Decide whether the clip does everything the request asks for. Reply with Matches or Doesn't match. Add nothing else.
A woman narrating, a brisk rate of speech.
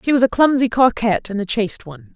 Matches